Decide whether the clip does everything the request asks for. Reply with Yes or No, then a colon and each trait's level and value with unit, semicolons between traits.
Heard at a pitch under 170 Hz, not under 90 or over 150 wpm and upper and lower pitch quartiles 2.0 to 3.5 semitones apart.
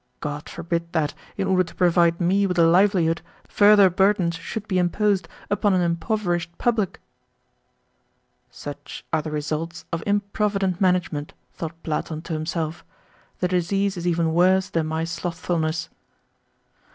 No: medium, 175 Hz; average, 140 wpm; average, 2.7 semitones